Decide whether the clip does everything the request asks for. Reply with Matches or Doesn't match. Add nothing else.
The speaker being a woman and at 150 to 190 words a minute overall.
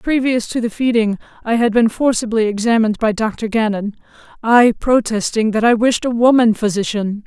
Matches